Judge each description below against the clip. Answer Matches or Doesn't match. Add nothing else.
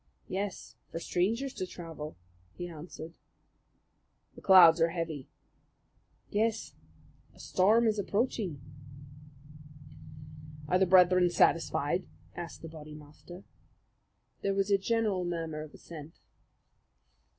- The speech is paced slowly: Matches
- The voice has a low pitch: Doesn't match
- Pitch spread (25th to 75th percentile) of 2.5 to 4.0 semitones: Matches